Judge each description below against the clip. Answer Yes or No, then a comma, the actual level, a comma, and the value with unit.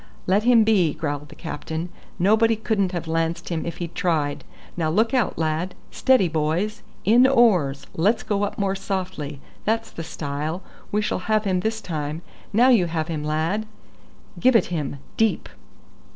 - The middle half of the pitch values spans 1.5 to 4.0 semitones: No, average, 5.3 semitones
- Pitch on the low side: No, medium, 180 Hz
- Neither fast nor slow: Yes, average, 165 wpm